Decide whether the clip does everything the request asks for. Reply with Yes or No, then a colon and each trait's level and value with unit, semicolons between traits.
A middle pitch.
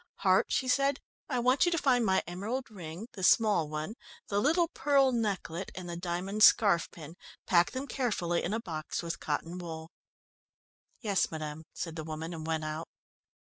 Yes: medium, 180 Hz